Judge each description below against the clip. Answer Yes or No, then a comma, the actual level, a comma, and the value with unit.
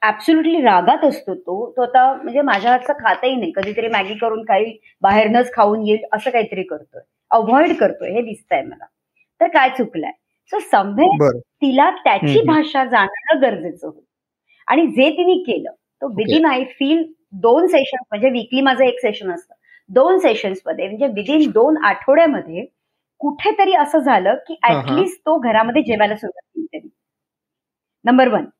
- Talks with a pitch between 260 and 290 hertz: Yes, very high, 265 Hz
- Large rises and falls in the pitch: Yes, wide, 6.3 semitones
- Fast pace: Yes, fast, 135 wpm